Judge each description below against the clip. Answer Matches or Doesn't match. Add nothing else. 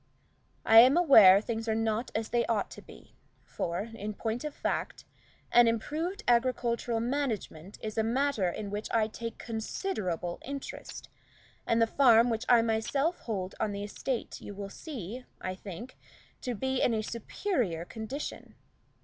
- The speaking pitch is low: Doesn't match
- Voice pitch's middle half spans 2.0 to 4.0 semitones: Matches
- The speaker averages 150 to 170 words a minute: Matches